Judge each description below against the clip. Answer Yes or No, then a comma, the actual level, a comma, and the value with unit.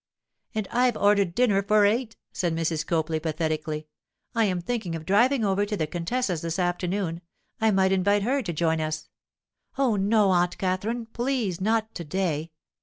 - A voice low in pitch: No, high, 190 Hz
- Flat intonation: No, average, 4.7 semitones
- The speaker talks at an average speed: Yes, average, 165 wpm